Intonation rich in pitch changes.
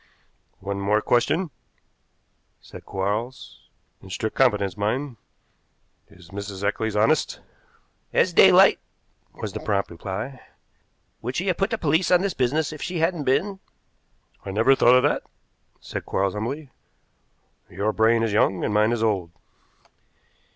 Yes: wide, 6.2 semitones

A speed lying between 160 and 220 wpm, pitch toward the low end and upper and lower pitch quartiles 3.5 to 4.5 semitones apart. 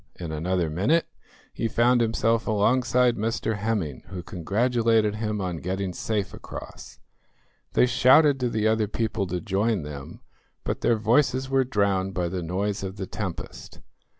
No: average, 150 wpm; low, 105 Hz; average, 3.9 semitones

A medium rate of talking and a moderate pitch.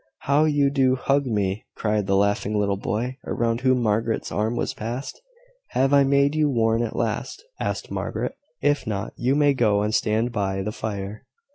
No: average, 180 wpm; low, 115 Hz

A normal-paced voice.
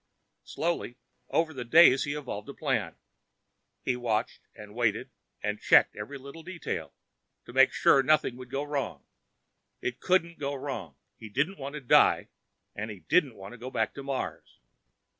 Yes: average, 165 wpm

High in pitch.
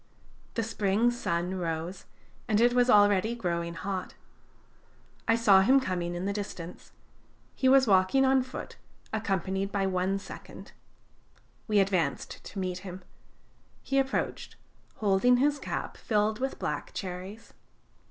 Yes: high, 200 Hz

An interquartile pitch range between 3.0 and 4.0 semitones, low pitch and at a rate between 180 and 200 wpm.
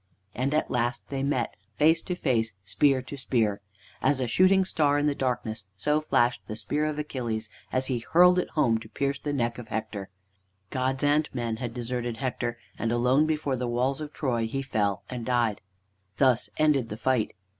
Yes: average, 3.7 semitones; low, 130 Hz; average, 190 wpm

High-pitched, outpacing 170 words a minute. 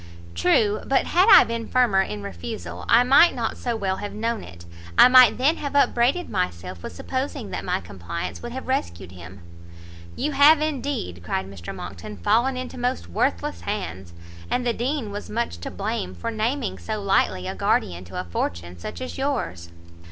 Yes: high, 200 Hz; average, 180 wpm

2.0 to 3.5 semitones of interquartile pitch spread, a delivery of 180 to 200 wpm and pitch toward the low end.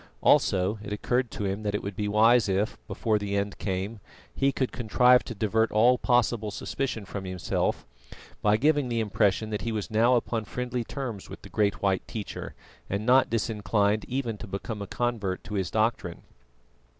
Yes: average, 3.0 semitones; average, 185 wpm; low, 110 Hz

